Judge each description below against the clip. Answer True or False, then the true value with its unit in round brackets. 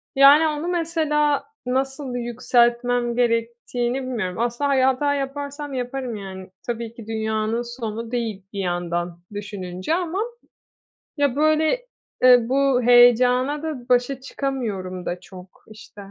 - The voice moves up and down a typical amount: True (4.0 semitones)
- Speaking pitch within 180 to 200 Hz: False (245 Hz)